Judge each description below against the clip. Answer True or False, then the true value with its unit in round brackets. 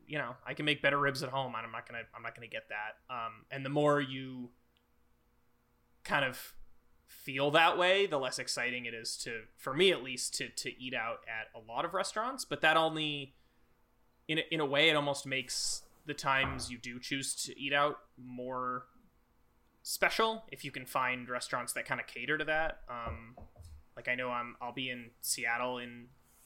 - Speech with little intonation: False (3.5 semitones)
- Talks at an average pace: True (195 wpm)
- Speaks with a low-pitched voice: True (130 Hz)